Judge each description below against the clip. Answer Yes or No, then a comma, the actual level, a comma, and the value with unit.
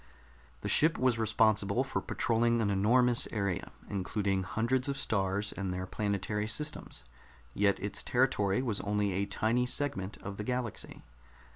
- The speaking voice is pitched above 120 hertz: No, low, 105 Hz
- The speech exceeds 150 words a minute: No, average, 145 wpm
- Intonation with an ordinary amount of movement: Yes, average, 3.7 semitones